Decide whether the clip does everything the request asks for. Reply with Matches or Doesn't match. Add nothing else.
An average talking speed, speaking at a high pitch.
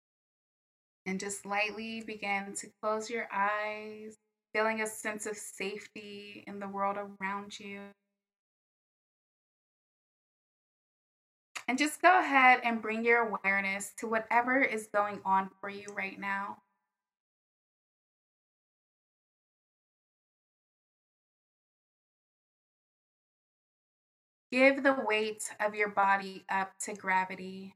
Doesn't match